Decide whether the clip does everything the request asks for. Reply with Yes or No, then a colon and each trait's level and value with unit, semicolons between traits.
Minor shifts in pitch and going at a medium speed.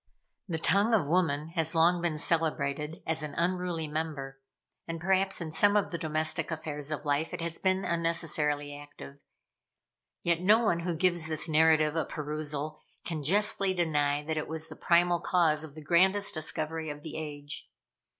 Yes: narrow, 2.3 semitones; average, 170 wpm